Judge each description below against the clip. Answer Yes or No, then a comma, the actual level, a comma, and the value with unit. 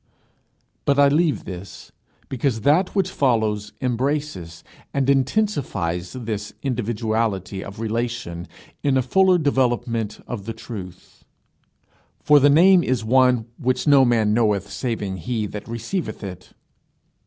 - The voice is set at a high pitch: No, low, 120 Hz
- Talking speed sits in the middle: No, slow, 125 wpm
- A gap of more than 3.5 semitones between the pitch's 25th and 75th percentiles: Yes, average, 4.9 semitones